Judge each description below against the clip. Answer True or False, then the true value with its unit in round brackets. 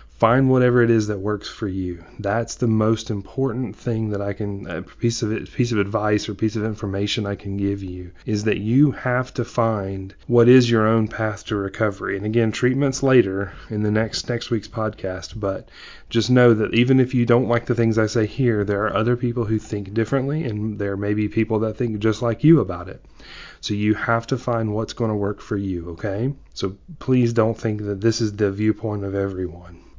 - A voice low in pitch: True (110 Hz)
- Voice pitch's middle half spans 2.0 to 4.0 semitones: True (2.8 semitones)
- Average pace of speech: False (220 wpm)